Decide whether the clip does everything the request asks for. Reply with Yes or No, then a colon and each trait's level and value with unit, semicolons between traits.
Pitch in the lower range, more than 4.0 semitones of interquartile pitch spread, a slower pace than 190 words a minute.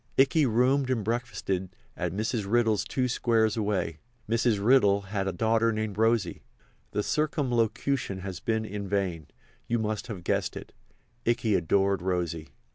No: low, 110 Hz; average, 3.4 semitones; slow, 135 wpm